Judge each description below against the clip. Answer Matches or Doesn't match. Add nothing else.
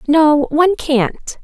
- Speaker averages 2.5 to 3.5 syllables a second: Matches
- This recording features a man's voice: Doesn't match